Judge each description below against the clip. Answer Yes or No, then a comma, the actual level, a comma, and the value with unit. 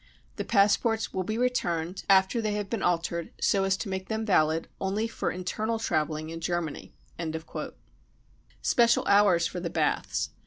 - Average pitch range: Yes, average, 4.3 semitones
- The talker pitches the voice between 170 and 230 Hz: Yes, high, 190 Hz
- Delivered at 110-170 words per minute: Yes, average, 155 wpm